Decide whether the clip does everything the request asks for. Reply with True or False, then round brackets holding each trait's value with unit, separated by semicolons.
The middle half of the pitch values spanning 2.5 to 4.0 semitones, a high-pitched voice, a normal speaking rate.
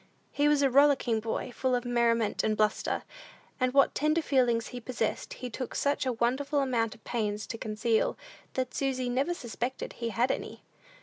True (2.9 semitones; 245 Hz; 180 wpm)